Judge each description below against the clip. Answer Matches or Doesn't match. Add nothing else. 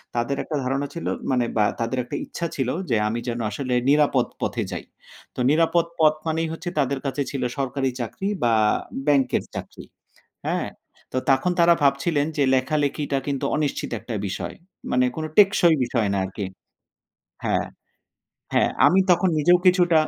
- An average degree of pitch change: Matches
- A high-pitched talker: Doesn't match